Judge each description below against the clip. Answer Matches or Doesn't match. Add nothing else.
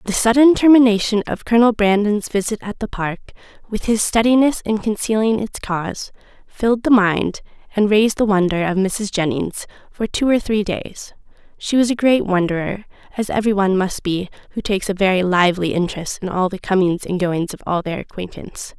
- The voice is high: Matches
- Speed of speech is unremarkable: Matches